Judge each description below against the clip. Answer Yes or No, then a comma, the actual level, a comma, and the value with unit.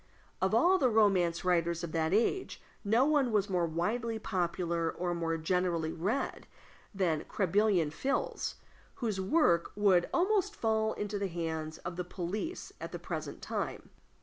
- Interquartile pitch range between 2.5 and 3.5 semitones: No, average, 4.5 semitones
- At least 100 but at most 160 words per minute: Yes, average, 150 wpm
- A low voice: No, medium, 185 Hz